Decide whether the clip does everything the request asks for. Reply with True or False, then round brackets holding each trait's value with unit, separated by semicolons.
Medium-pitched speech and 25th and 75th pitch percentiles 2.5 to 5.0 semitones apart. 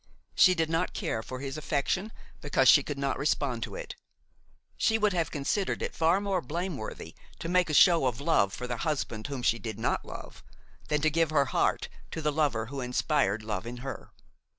False (150 Hz; 5.4 semitones)